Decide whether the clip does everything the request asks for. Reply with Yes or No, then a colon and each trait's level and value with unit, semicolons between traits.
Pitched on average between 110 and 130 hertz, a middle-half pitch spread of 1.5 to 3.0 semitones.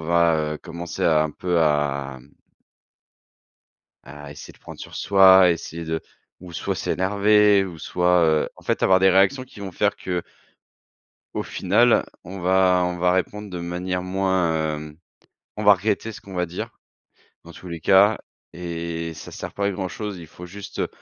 No: very low, 90 Hz; average, 2.7 semitones